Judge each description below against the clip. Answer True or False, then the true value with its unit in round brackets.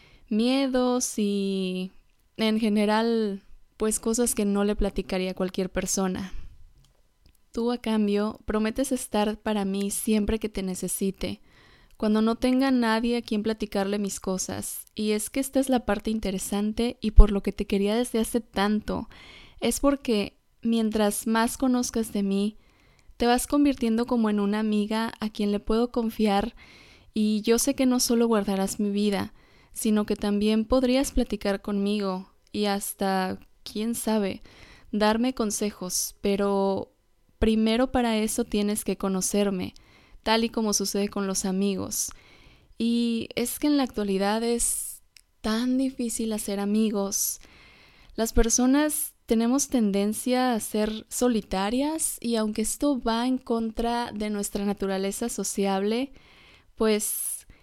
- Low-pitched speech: False (215 Hz)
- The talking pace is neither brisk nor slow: True (140 wpm)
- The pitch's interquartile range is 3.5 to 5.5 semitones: False (2.7 semitones)